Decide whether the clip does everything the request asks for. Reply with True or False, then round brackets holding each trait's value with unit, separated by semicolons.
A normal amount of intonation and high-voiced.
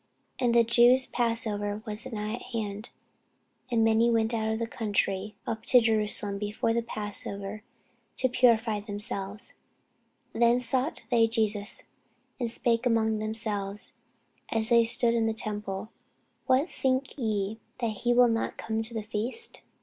False (2.0 semitones; 225 Hz)